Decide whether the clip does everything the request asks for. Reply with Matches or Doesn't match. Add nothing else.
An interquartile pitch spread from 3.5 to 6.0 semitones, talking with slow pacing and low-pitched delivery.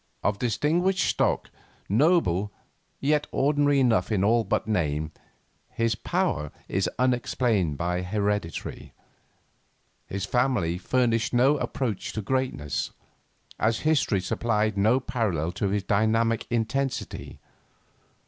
Matches